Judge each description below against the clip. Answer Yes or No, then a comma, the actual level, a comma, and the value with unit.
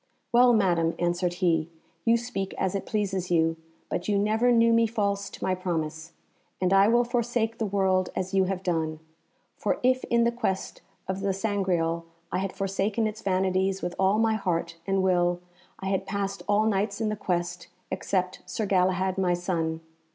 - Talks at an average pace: Yes, average, 180 wpm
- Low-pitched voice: No, high, 190 Hz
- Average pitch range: Yes, average, 3.0 semitones